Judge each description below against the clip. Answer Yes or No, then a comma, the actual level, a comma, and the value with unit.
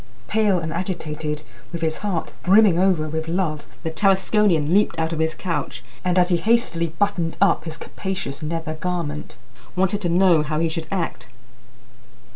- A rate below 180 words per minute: Yes, average, 165 wpm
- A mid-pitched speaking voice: Yes, medium, 170 Hz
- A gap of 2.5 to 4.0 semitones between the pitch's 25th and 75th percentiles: Yes, average, 3.0 semitones